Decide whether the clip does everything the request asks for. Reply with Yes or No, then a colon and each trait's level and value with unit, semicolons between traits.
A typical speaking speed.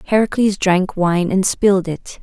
Yes: average, 160 wpm